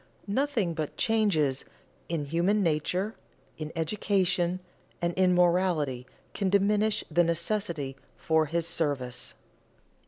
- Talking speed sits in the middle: No, slow, 105 wpm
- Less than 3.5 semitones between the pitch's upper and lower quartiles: No, average, 4.3 semitones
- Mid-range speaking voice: Yes, medium, 175 Hz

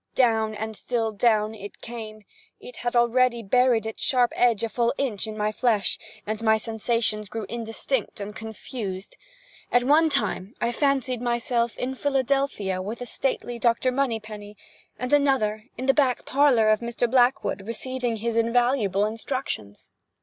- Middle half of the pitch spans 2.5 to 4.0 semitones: Yes, average, 2.8 semitones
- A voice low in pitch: No, high, 235 Hz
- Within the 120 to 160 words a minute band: Yes, average, 155 wpm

